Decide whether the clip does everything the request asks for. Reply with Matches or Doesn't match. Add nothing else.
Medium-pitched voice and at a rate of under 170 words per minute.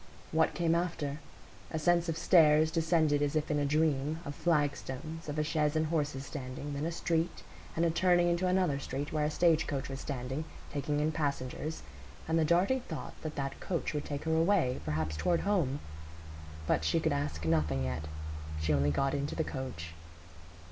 Doesn't match